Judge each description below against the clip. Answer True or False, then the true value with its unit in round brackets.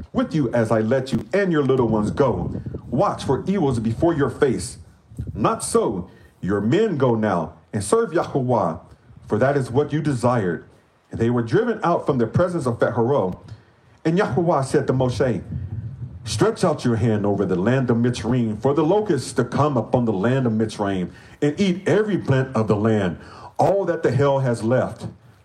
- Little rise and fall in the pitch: False (5.0 semitones)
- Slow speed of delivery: False (185 wpm)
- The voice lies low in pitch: True (125 Hz)